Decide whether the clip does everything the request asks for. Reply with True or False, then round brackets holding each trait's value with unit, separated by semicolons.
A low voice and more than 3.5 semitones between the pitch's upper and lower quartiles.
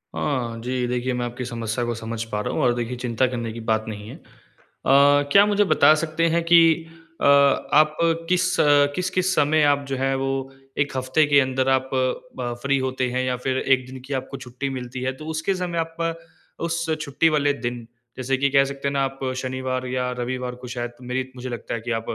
False (130 Hz; 2.7 semitones)